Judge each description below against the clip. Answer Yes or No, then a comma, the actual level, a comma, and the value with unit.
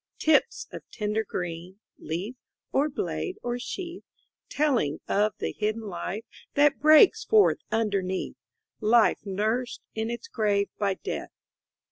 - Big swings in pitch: Yes, wide, 5.8 semitones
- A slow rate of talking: Yes, slow, 125 wpm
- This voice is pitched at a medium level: No, high, 220 Hz